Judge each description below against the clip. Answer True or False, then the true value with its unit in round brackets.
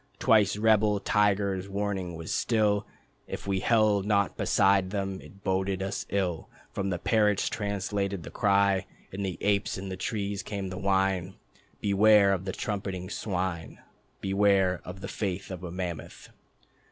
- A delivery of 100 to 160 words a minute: True (155 wpm)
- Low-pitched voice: True (100 Hz)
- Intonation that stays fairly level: True (1.5 semitones)